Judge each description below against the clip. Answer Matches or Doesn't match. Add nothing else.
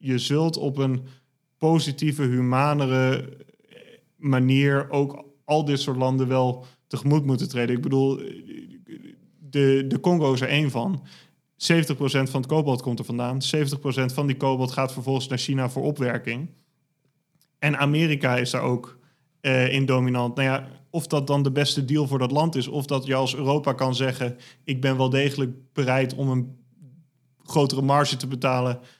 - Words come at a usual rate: Matches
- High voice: Doesn't match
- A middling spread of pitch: Doesn't match